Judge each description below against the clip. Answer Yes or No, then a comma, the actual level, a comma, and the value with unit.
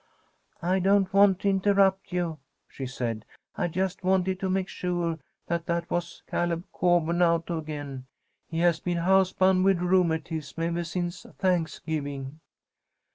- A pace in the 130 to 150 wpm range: Yes, average, 140 wpm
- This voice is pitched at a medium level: Yes, medium, 175 Hz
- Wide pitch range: No, narrow, 2.6 semitones